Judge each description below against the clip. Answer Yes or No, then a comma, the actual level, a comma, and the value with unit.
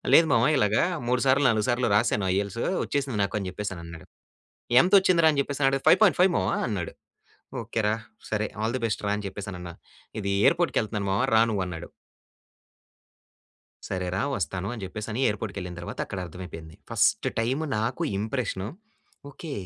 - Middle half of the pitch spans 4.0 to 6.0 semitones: Yes, average, 4.9 semitones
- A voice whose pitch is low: Yes, low, 105 Hz